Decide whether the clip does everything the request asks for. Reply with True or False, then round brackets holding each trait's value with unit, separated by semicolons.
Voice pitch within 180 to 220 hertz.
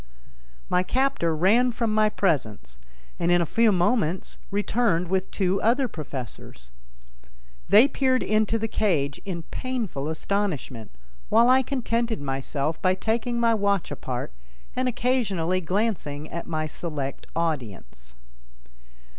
True (185 Hz)